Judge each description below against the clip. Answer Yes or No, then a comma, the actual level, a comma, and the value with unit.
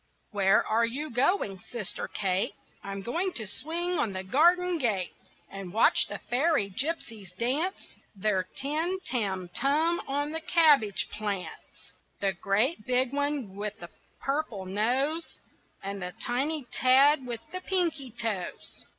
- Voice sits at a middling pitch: No, high, 245 Hz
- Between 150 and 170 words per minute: No, average, 140 wpm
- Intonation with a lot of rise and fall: Yes, wide, 7.5 semitones